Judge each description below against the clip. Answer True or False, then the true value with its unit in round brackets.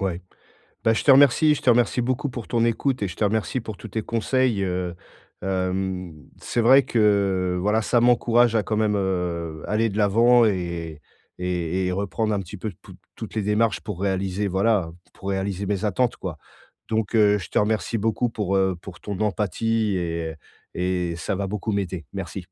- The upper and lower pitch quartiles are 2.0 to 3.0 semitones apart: False (3.5 semitones)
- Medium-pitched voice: False (100 Hz)